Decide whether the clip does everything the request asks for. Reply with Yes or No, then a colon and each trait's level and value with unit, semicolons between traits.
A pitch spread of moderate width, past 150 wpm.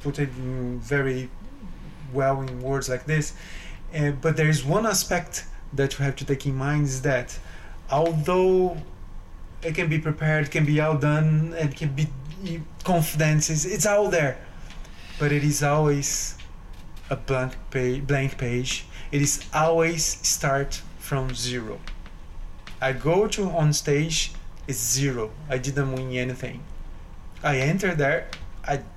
No: average, 3.5 semitones; average, 140 wpm